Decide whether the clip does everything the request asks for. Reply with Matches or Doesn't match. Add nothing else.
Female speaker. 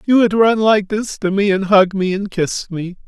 Doesn't match